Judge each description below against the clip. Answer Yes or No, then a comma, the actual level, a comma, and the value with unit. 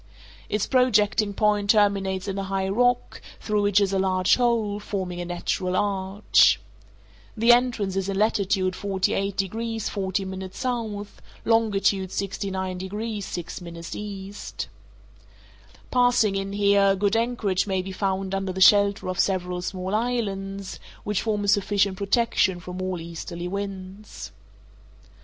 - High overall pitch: Yes, high, 195 Hz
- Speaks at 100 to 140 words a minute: Yes, slow, 135 wpm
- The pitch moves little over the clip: Yes, narrow, 1.8 semitones